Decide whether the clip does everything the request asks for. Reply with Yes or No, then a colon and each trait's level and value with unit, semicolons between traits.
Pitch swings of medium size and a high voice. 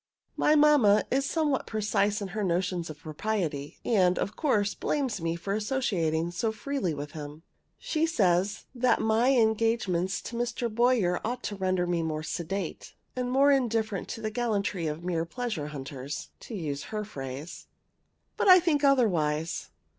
No: wide, 6.2 semitones; high, 205 Hz